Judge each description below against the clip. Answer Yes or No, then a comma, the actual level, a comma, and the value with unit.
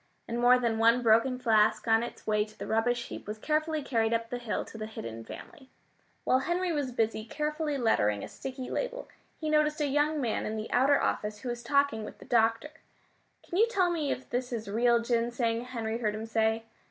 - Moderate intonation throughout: Yes, average, 4.1 semitones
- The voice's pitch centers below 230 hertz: No, high, 240 Hz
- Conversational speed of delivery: No, fast, 215 wpm